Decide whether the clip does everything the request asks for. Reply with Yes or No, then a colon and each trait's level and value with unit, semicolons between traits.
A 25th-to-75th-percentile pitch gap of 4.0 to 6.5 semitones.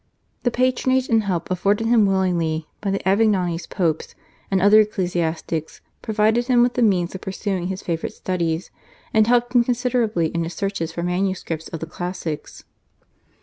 Yes: average, 4.5 semitones